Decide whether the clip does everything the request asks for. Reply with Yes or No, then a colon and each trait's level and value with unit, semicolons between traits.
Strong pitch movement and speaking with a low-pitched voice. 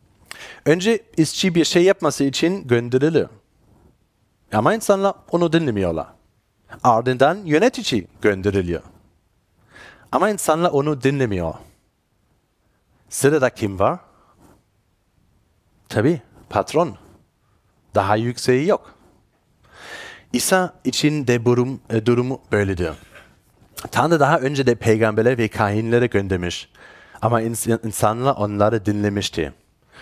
Yes: wide, 5.9 semitones; low, 115 Hz